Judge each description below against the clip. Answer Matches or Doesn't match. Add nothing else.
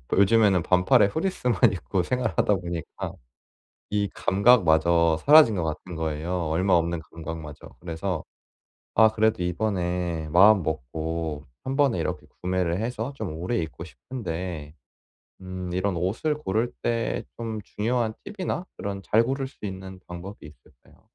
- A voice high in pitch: Doesn't match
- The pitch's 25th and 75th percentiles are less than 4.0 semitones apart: Doesn't match